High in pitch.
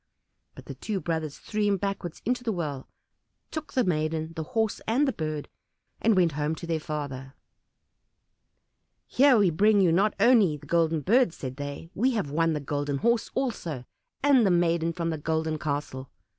No: medium, 165 Hz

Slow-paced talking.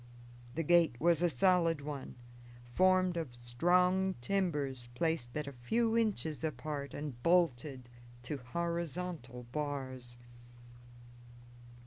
Yes: slow, 105 wpm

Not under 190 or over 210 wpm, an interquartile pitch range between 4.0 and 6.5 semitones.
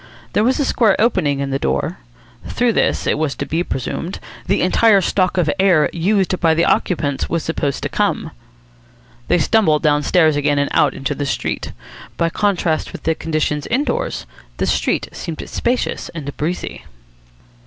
No: average, 165 wpm; average, 4.6 semitones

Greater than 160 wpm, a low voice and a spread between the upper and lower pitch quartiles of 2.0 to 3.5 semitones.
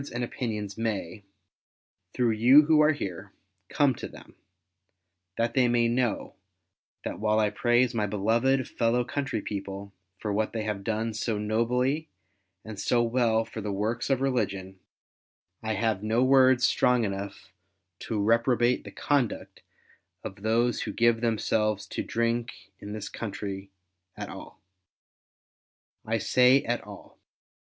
No: average, 140 wpm; low, 115 Hz; average, 2.8 semitones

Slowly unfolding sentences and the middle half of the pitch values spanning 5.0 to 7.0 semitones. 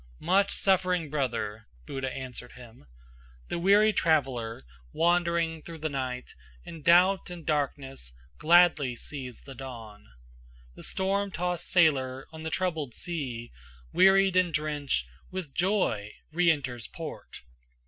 Yes: slow, 125 wpm; wide, 5.5 semitones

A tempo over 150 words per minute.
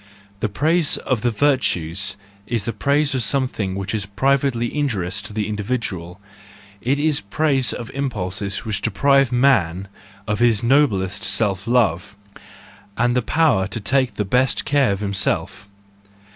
No: average, 145 wpm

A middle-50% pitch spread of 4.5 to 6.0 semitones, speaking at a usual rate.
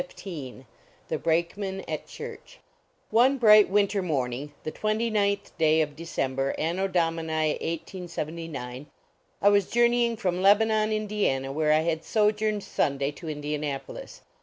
Yes: wide, 5.6 semitones; average, 150 wpm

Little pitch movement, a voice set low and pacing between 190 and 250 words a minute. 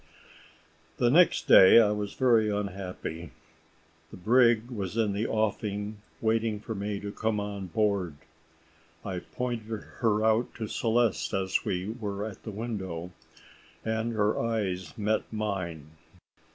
No: narrow, 2.2 semitones; low, 105 Hz; slow, 135 wpm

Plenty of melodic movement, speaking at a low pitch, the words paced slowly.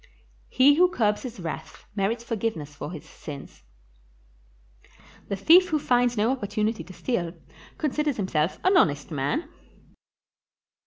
No: wide, 7.5 semitones; high, 220 Hz; slow, 125 wpm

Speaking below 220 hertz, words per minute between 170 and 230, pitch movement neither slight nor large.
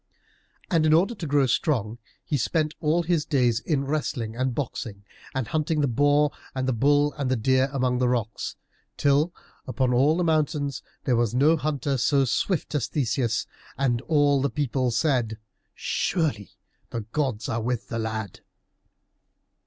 No: low, 135 Hz; average, 160 wpm; average, 3.8 semitones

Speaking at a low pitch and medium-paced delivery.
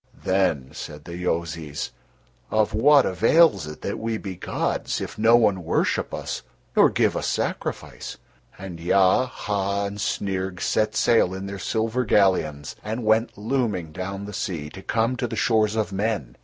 Yes: low, 100 Hz; average, 165 wpm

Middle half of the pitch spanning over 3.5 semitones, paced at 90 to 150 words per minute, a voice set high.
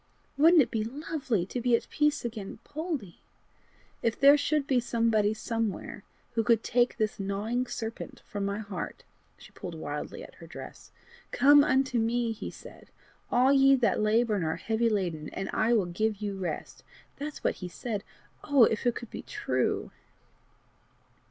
No: average, 4.2 semitones; average, 170 wpm; high, 230 Hz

